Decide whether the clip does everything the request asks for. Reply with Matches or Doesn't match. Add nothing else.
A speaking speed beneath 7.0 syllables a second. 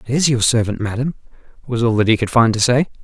Doesn't match